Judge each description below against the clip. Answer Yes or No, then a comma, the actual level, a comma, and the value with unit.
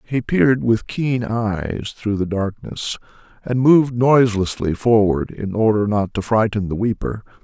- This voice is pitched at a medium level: No, low, 110 Hz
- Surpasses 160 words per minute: No, average, 155 wpm